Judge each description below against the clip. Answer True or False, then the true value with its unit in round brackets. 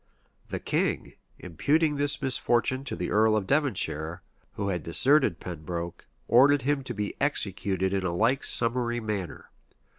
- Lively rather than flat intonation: True (6.6 semitones)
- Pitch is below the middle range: True (110 Hz)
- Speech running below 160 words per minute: True (145 wpm)